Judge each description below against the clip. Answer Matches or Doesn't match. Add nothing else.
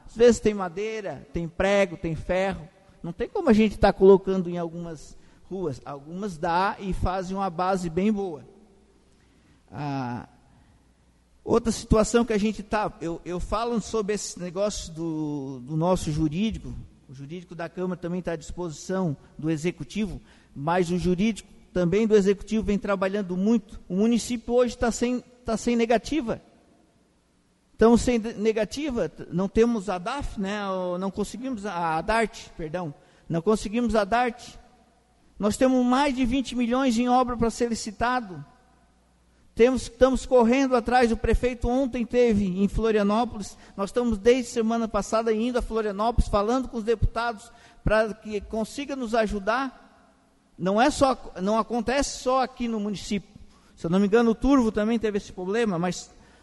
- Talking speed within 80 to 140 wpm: Doesn't match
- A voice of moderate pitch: Doesn't match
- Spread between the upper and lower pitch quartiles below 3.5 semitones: Doesn't match